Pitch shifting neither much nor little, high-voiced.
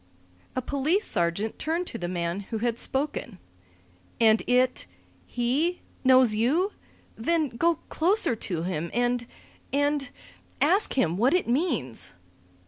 No: wide, 6.1 semitones; high, 245 Hz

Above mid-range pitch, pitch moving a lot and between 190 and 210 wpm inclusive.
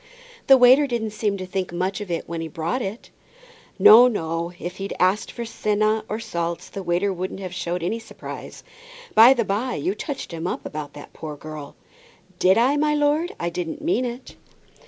Yes: high, 195 Hz; wide, 5.7 semitones; average, 195 wpm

